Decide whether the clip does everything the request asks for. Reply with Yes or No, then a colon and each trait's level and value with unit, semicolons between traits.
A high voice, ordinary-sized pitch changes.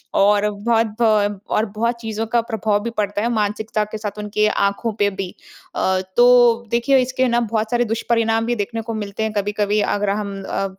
No: high, 215 Hz; narrow, 2.1 semitones